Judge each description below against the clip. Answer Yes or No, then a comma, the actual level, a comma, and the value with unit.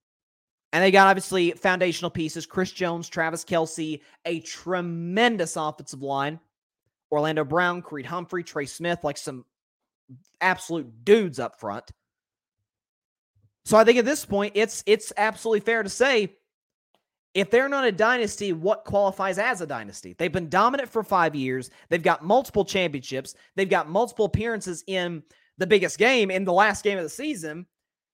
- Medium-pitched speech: Yes, medium, 180 Hz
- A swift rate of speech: No, average, 155 wpm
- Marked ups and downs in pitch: No, average, 4.7 semitones